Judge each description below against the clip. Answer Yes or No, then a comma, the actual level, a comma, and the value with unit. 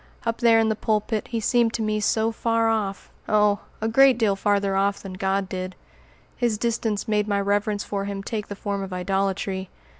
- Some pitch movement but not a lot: No, narrow, 2.2 semitones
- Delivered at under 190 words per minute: No, average, 200 wpm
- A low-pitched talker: No, high, 210 Hz